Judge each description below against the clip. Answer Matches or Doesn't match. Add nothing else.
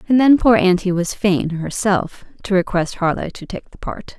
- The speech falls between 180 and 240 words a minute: Matches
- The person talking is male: Doesn't match